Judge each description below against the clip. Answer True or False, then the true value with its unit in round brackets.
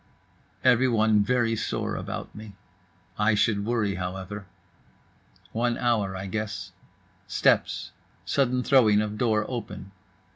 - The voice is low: True (110 Hz)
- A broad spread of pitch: False (2.9 semitones)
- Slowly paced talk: True (110 wpm)